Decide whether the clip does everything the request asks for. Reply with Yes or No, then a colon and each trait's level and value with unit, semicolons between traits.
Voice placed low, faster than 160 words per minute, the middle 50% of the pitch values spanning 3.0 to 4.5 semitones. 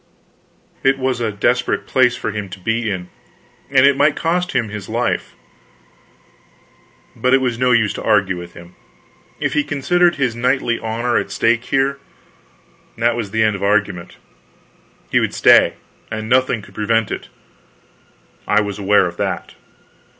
No: low, 115 Hz; average, 155 wpm; average, 4.0 semitones